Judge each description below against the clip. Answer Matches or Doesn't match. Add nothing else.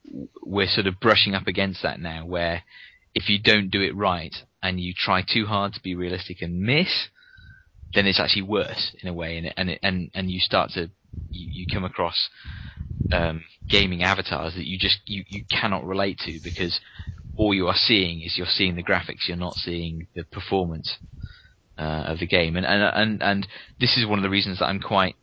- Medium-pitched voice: Doesn't match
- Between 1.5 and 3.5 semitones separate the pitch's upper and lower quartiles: Matches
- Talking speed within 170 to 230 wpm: Matches